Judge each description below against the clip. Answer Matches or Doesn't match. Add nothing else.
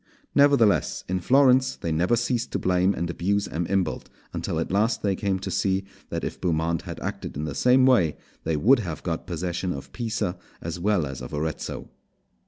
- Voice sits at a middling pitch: Doesn't match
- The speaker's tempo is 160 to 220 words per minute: Matches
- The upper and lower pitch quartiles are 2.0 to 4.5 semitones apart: Doesn't match